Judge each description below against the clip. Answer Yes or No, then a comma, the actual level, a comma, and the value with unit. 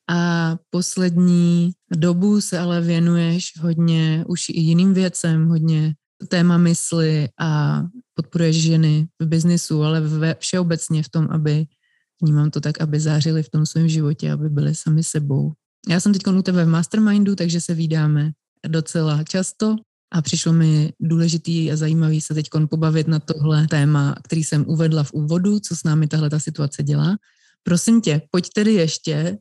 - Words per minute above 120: Yes, average, 160 wpm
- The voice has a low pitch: No, medium, 165 Hz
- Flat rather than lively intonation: Yes, narrow, 2.0 semitones